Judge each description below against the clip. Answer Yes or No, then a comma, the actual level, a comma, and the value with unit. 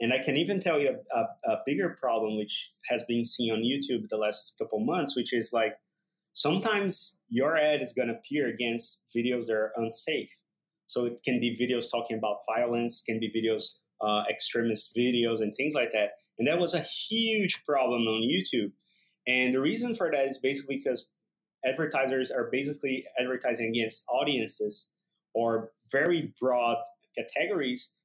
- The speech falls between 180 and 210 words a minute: No, average, 170 wpm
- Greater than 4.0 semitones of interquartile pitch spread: Yes, average, 4.4 semitones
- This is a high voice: No, low, 125 Hz